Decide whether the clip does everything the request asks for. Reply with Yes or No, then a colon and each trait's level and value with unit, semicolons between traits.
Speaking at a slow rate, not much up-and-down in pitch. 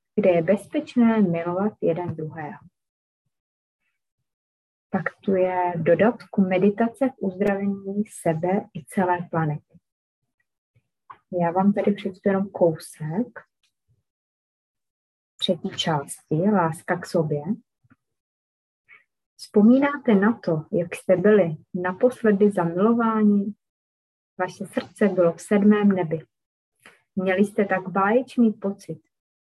No: slow, 95 wpm; average, 4.2 semitones